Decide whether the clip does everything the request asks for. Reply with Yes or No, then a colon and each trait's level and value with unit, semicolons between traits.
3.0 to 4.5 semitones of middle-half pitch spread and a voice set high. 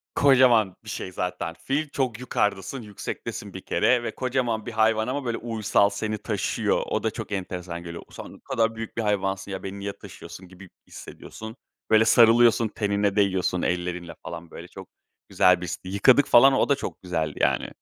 No: average, 4.1 semitones; low, 105 Hz